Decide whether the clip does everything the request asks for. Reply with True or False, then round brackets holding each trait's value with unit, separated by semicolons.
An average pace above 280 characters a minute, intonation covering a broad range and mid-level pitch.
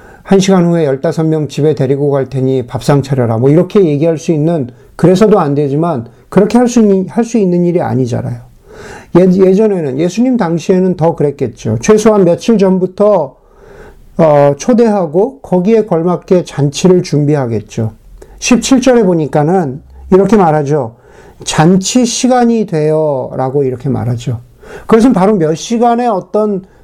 True (300 characters per minute; 6.4 semitones; 170 Hz)